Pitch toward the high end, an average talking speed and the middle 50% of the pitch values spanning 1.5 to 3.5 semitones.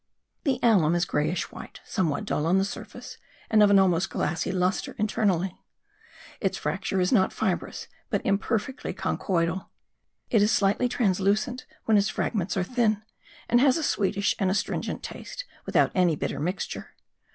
Yes: high, 195 Hz; average, 155 wpm; average, 3.2 semitones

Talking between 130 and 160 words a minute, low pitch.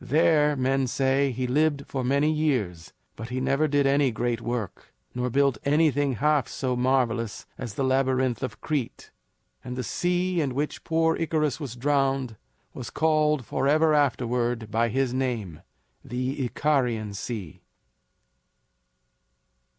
Yes: slow, 135 wpm; low, 130 Hz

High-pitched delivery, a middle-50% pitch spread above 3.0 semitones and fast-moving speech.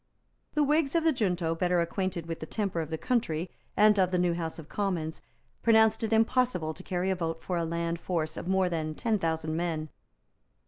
No: medium, 180 Hz; average, 4.3 semitones; fast, 210 wpm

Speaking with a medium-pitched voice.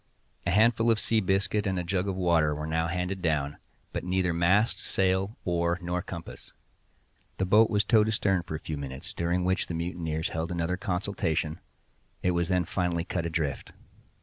No: very low, 90 Hz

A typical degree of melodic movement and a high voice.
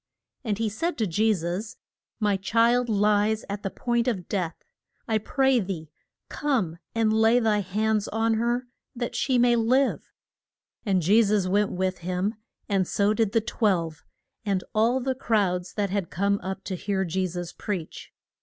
Yes: average, 3.3 semitones; high, 210 Hz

